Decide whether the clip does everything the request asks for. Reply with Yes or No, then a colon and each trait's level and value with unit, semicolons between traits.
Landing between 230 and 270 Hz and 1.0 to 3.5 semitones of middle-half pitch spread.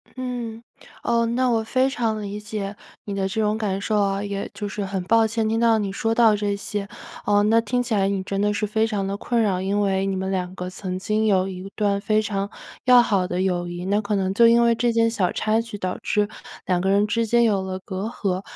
No: high, 205 Hz; narrow, 2.6 semitones